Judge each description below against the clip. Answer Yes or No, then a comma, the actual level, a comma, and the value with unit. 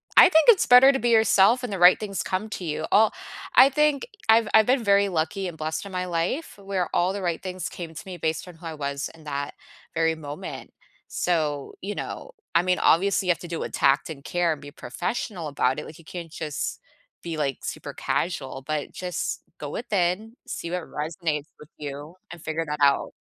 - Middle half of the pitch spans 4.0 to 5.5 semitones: Yes, average, 4.4 semitones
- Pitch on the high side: No, medium, 175 Hz